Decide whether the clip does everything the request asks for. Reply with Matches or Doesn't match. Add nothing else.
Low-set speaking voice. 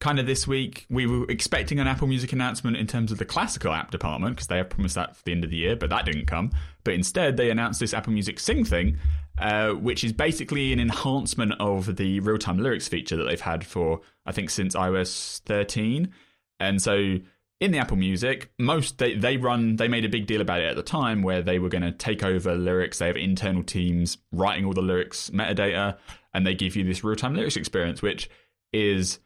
Matches